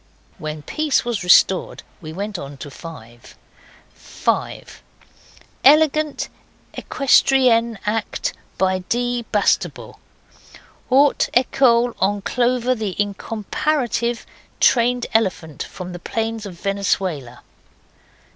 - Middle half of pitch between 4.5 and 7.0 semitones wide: Yes, average, 5.0 semitones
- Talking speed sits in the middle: No, slow, 95 wpm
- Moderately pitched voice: No, high, 220 Hz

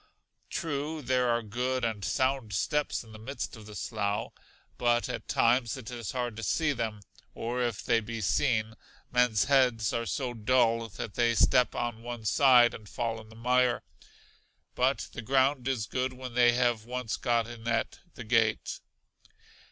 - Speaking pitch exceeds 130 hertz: No, low, 120 Hz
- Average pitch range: No, narrow, 2.1 semitones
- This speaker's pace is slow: No, average, 175 wpm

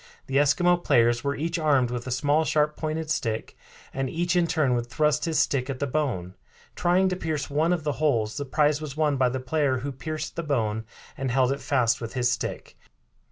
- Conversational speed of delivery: No, fast, 215 wpm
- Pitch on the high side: No, medium, 145 Hz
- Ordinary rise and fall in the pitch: Yes, average, 3.6 semitones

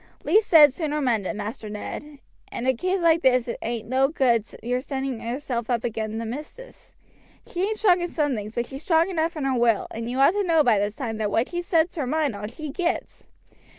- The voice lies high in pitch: Yes, very high, 265 Hz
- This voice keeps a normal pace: No, fast, 225 wpm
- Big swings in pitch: Yes, wide, 5.8 semitones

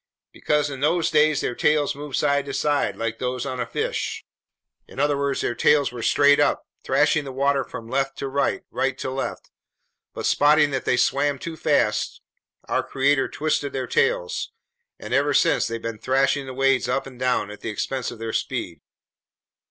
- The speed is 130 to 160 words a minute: No, average, 185 wpm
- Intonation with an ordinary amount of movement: No, narrow, 2.3 semitones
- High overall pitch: No, low, 135 Hz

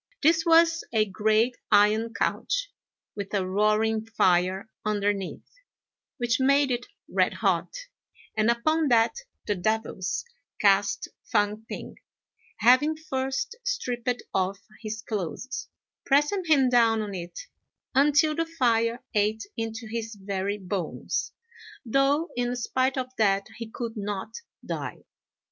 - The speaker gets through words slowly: Yes, slow, 120 wpm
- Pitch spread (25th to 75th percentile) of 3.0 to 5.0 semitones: Yes, average, 4.3 semitones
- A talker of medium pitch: No, high, 225 Hz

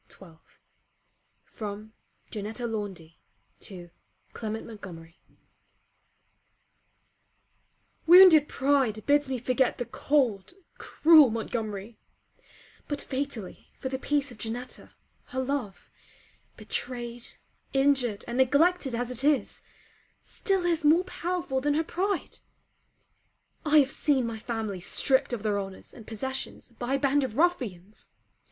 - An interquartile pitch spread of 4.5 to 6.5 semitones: Yes, average, 4.8 semitones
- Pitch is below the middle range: No, very high, 250 Hz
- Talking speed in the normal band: No, slow, 120 wpm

